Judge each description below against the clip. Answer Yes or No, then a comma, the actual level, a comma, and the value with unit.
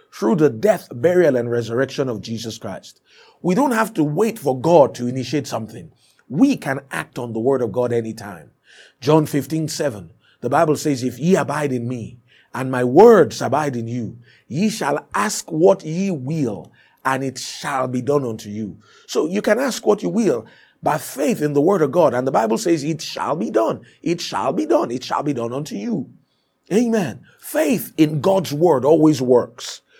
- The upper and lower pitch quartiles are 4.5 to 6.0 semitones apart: Yes, wide, 5.5 semitones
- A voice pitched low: No, medium, 145 Hz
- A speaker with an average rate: Yes, average, 190 wpm